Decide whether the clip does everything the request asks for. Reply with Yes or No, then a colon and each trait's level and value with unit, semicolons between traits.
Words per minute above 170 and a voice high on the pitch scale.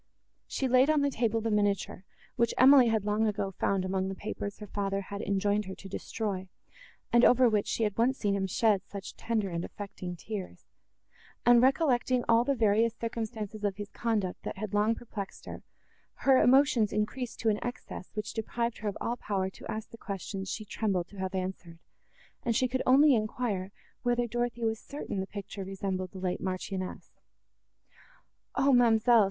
Yes: average, 180 wpm; high, 215 Hz